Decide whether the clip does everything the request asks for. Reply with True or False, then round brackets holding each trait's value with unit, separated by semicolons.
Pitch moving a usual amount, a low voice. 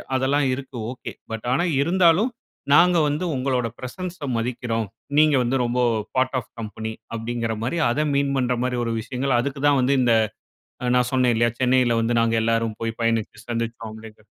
True (3.2 semitones; 125 Hz)